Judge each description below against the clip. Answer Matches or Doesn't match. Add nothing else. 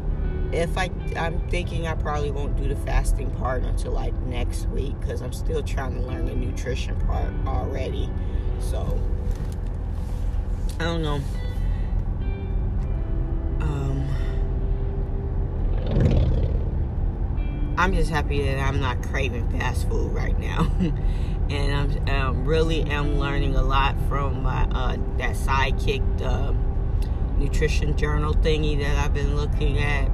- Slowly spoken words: Matches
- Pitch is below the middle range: Matches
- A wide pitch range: Doesn't match